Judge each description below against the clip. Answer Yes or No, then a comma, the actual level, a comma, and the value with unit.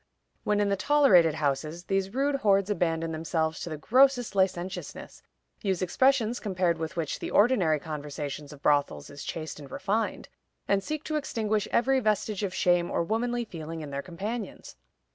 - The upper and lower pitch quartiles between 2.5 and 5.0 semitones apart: No, wide, 5.4 semitones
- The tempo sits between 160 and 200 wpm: Yes, average, 165 wpm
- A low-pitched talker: No, high, 190 Hz